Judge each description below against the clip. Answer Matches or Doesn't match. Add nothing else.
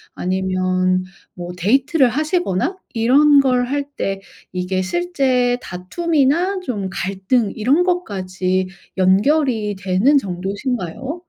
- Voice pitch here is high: Matches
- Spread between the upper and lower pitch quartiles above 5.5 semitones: Matches